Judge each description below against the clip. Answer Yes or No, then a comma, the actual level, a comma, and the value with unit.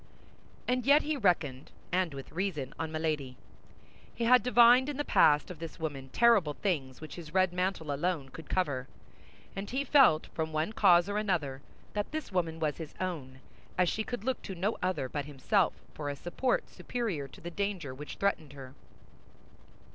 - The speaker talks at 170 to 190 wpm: Yes, average, 180 wpm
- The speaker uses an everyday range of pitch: No, wide, 5.7 semitones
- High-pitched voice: No, medium, 175 Hz